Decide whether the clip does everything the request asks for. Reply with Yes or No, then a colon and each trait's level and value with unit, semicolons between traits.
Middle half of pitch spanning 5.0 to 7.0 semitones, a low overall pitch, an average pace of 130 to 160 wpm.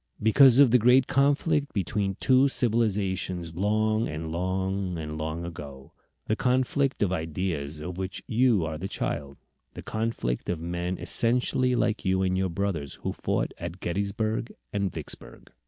Yes: average, 5.3 semitones; very low, 95 Hz; average, 155 wpm